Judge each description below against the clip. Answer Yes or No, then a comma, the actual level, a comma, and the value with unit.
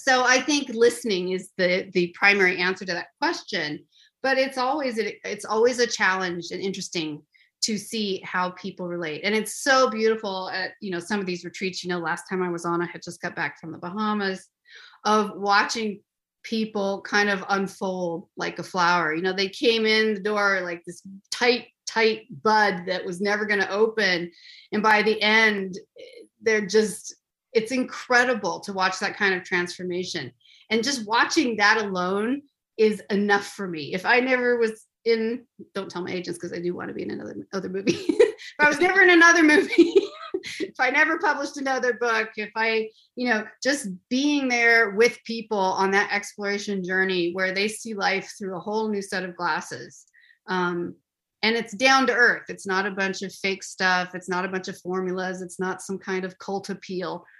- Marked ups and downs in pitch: No, average, 4.0 semitones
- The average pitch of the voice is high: Yes, high, 205 Hz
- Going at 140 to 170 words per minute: No, average, 190 wpm